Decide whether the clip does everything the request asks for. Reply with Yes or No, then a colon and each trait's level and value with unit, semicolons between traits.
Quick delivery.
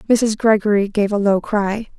No: average, 180 wpm